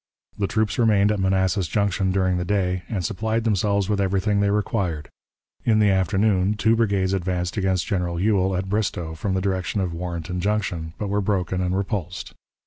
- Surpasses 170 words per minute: Yes, average, 180 wpm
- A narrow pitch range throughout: Yes, narrow, 2.2 semitones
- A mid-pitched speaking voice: No, very low, 95 Hz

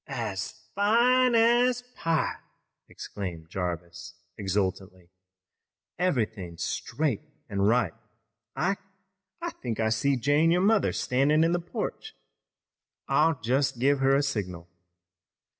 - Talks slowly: Yes, slow, 110 wpm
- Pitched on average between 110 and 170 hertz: Yes, low, 135 Hz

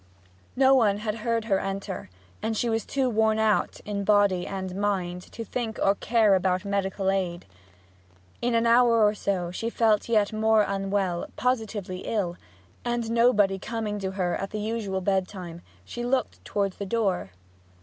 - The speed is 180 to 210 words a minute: No, average, 165 wpm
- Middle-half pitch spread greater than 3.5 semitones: No, average, 2.8 semitones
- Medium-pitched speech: No, high, 205 Hz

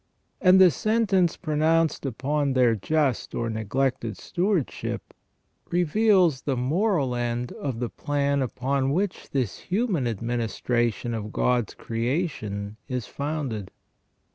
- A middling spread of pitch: No, wide, 5.7 semitones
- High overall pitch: No, low, 135 Hz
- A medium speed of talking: No, slow, 115 wpm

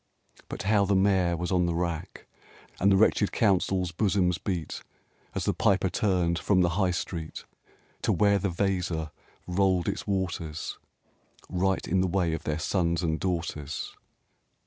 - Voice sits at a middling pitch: No, very low, 90 Hz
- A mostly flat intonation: Yes, narrow, 2.3 semitones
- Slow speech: No, average, 155 wpm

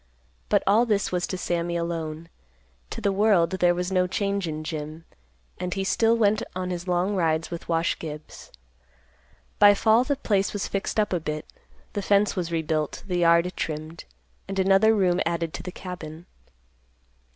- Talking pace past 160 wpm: Yes, average, 175 wpm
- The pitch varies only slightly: No, average, 3.1 semitones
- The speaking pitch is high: No, medium, 180 Hz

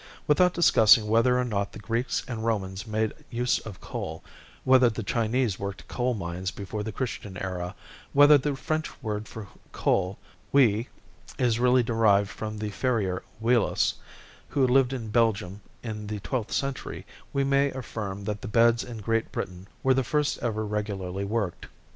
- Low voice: Yes, low, 110 Hz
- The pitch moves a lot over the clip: No, average, 3.6 semitones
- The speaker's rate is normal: Yes, average, 165 wpm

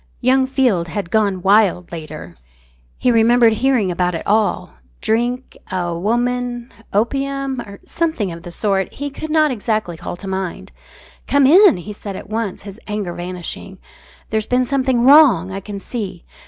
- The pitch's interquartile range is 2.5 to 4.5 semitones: No, average, 5.2 semitones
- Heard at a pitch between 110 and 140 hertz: No, high, 215 Hz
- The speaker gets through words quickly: No, average, 160 wpm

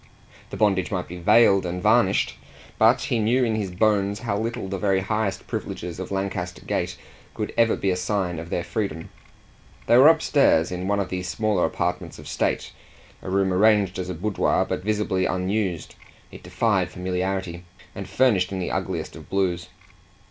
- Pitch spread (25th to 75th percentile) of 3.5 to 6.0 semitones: No, average, 2.8 semitones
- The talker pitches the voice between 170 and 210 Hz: No, very low, 95 Hz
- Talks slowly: No, average, 175 wpm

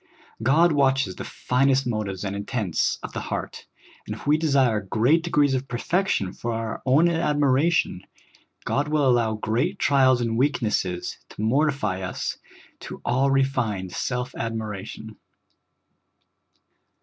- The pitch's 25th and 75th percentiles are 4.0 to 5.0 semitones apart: Yes, average, 4.5 semitones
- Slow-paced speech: Yes, slow, 130 wpm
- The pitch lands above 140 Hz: No, low, 125 Hz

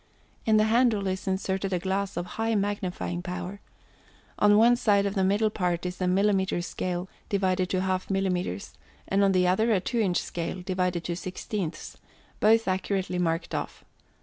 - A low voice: No, high, 190 Hz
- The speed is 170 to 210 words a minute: Yes, average, 175 wpm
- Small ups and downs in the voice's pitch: Yes, narrow, 2.1 semitones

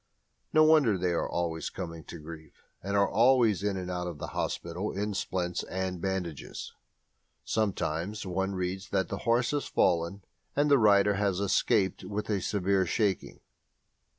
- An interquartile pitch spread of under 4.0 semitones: Yes, average, 2.7 semitones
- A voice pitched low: Yes, very low, 95 Hz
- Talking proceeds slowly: No, average, 155 wpm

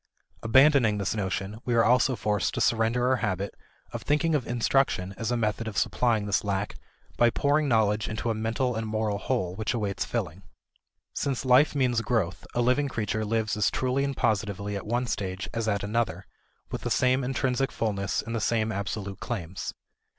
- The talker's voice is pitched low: Yes, low, 110 Hz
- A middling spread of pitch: Yes, average, 3.3 semitones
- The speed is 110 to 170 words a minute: No, average, 185 wpm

